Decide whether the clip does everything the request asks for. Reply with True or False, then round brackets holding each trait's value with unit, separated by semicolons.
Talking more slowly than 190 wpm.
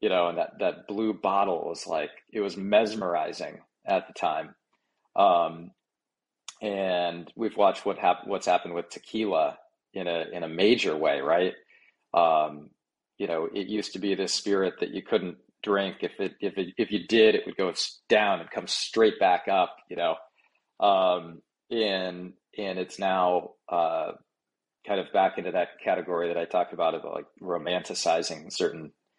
True (170 wpm)